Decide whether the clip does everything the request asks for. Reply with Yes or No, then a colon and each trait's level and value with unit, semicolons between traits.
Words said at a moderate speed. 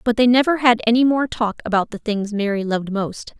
No: fast, 230 wpm